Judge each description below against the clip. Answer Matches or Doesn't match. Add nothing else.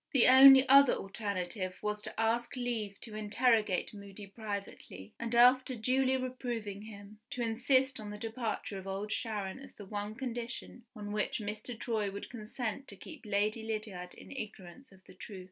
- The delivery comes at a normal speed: Matches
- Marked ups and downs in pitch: Doesn't match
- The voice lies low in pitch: Doesn't match